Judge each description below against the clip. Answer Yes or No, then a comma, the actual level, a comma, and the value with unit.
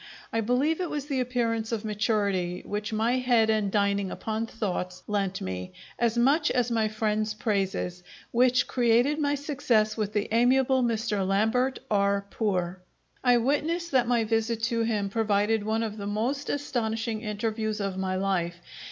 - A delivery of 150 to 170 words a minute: Yes, average, 160 wpm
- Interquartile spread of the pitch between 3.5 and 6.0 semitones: No, average, 3.1 semitones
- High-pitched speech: Yes, high, 220 Hz